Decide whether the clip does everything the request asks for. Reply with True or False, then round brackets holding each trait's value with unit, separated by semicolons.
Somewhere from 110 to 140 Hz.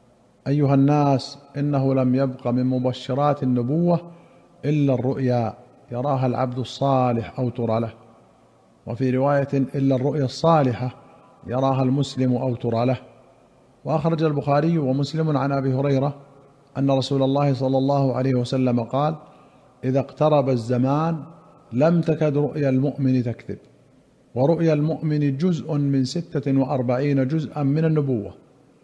True (135 Hz)